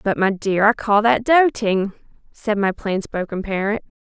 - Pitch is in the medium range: No, high, 210 Hz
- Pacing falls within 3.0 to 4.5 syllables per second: Yes, 4.4 syllables/s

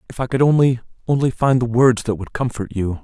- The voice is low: Yes, low, 120 Hz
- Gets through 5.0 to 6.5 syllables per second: Yes, 5.9 syllables/s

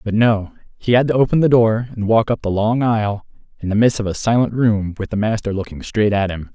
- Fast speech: Yes, fast, 255 wpm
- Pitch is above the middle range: No, low, 110 Hz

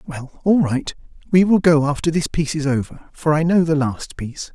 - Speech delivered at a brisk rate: Yes, fast, 225 wpm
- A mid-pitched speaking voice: Yes, medium, 155 Hz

